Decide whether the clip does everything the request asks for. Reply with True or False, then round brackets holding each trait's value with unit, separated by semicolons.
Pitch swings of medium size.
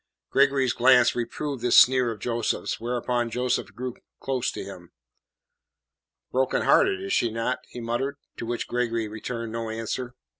False (1.8 semitones)